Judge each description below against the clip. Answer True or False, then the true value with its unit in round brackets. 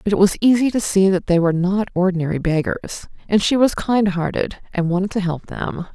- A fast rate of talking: True (220 wpm)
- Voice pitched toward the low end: False (190 Hz)